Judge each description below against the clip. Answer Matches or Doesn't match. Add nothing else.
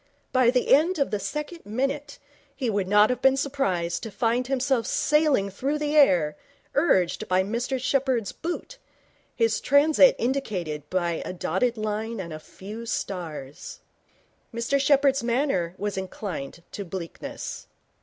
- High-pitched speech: Matches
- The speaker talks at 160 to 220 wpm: Doesn't match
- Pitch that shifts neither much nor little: Doesn't match